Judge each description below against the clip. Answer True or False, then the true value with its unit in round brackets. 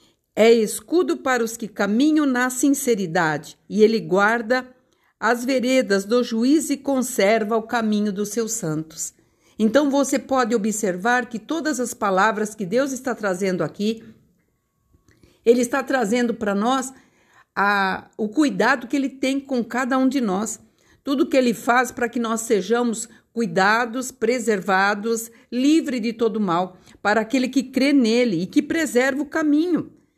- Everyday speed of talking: True (150 wpm)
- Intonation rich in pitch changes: False (3.6 semitones)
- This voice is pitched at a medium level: False (240 Hz)